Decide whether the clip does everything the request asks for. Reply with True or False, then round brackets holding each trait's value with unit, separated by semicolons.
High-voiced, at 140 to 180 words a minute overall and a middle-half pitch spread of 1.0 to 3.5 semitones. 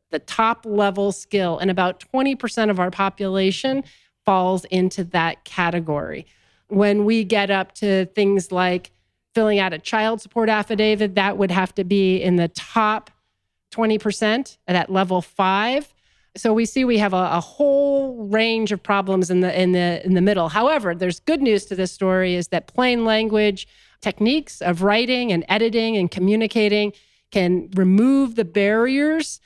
True (205 Hz; 160 wpm; 3.2 semitones)